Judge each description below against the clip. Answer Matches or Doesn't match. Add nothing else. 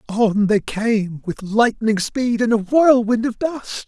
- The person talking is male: Matches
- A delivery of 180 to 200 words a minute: Doesn't match